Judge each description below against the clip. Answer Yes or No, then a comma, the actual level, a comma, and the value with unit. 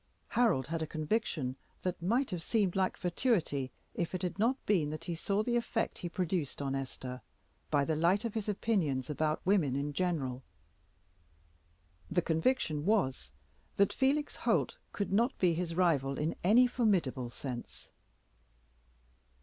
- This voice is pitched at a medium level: Yes, medium, 175 Hz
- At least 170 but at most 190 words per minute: No, average, 150 wpm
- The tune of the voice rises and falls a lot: Yes, wide, 6.2 semitones